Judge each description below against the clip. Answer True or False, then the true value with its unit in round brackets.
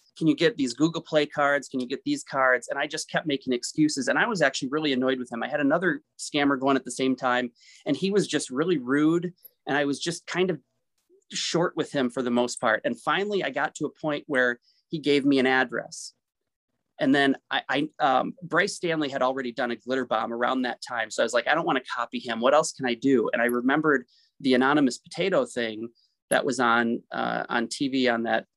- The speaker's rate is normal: False (235 wpm)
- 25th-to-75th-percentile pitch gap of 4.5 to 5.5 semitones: False (3.7 semitones)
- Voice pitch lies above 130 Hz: True (140 Hz)